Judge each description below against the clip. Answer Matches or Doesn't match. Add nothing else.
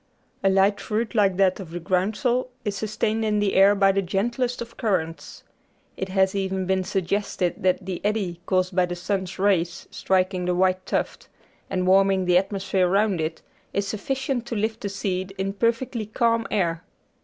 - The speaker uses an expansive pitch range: Doesn't match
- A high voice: Matches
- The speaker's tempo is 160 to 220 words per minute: Matches